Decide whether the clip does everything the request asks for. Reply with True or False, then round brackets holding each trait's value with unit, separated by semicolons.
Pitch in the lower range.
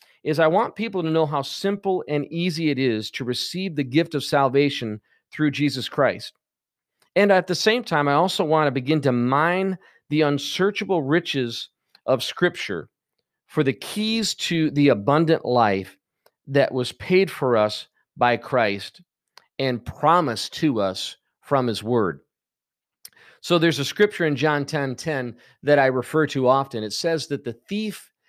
False (145 Hz)